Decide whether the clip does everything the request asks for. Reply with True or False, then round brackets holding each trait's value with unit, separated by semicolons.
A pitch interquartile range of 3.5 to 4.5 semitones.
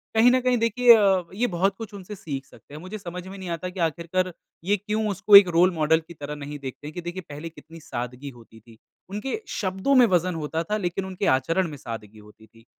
False (5.3 semitones)